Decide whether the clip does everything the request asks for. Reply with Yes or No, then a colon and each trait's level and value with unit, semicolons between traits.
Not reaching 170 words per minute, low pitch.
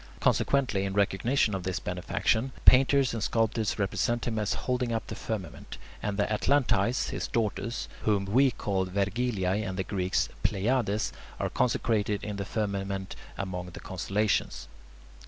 Yes: average, 150 wpm; low, 105 Hz